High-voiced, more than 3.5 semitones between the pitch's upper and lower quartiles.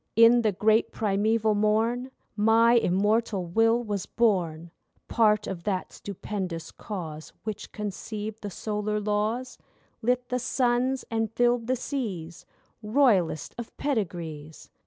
No: high, 215 Hz; average, 3.2 semitones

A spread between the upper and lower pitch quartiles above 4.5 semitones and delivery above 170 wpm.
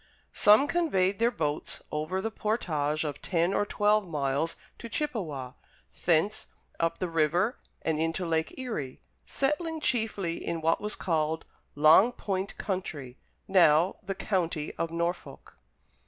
No: average, 5.1 semitones; slow, 135 wpm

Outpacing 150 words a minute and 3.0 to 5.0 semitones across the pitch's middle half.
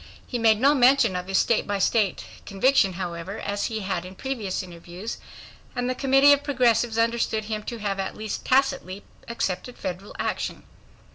Yes: average, 170 wpm; average, 4.5 semitones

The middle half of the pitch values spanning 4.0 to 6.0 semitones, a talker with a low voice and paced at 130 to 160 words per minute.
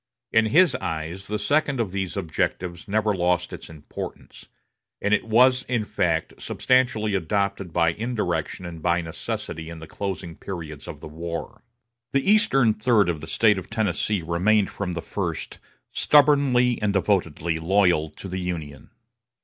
Yes: average, 4.7 semitones; very low, 95 Hz; average, 155 wpm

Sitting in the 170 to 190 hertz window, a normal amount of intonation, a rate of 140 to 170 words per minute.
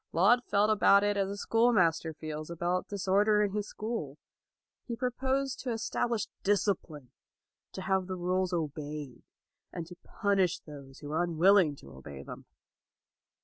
Yes: medium, 185 Hz; average, 5.0 semitones; average, 150 wpm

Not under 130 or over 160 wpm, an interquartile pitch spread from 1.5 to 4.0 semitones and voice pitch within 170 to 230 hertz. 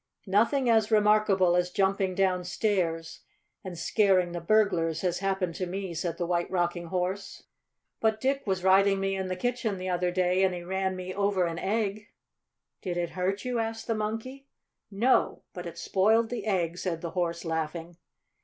No: average, 175 wpm; average, 3.1 semitones; high, 190 Hz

